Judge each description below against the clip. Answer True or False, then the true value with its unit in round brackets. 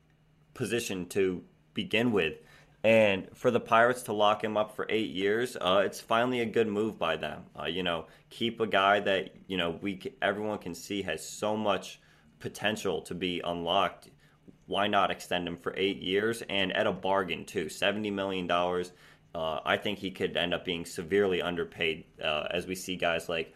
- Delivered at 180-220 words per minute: True (190 wpm)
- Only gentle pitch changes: False (3.7 semitones)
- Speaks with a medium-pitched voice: False (100 Hz)